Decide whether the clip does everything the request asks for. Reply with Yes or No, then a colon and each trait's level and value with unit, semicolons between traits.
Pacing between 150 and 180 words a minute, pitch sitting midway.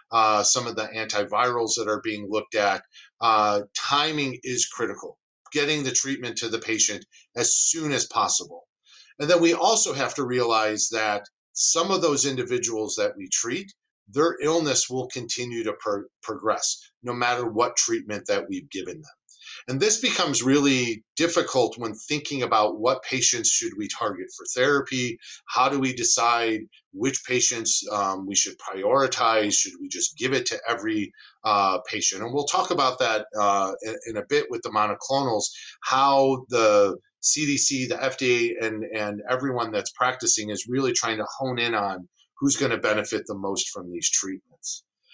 No: average, 165 wpm; low, 125 Hz